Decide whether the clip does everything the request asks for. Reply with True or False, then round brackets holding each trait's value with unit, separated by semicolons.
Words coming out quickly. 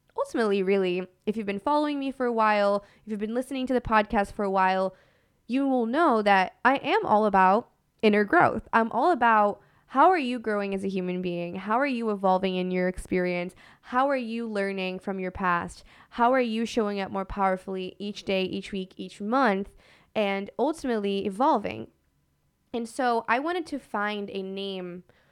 False (185 wpm)